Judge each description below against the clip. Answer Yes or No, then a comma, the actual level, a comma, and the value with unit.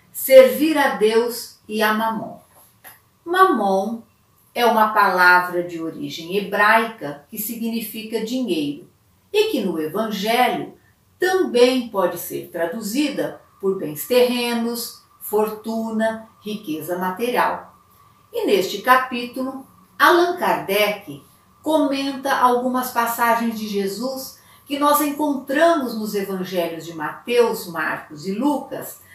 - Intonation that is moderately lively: Yes, average, 4.8 semitones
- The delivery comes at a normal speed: No, slow, 105 wpm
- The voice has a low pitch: No, high, 230 Hz